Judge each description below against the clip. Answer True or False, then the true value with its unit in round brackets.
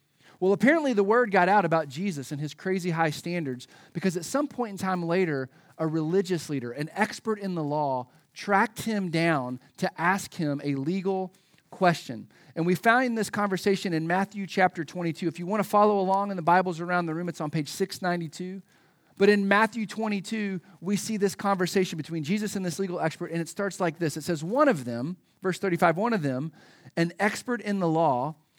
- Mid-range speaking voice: True (180 Hz)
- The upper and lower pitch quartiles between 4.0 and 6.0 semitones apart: False (3.6 semitones)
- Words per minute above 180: True (200 wpm)